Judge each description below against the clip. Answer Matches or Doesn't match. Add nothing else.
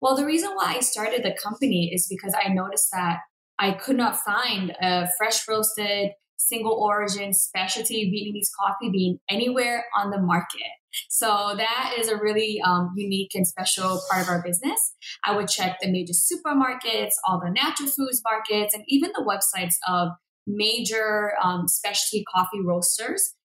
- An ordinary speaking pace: Matches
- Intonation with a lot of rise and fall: Doesn't match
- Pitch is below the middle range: Doesn't match